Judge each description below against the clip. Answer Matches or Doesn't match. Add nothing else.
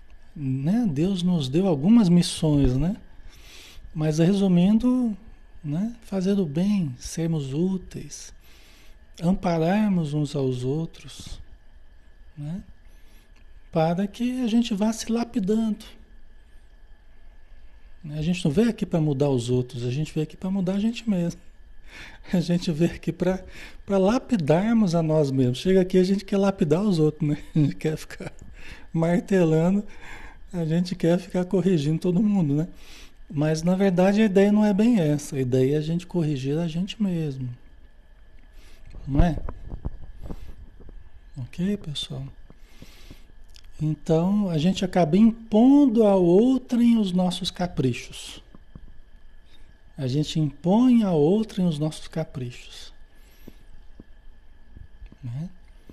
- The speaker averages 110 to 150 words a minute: Matches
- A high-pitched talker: Doesn't match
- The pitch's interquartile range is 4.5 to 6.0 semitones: Doesn't match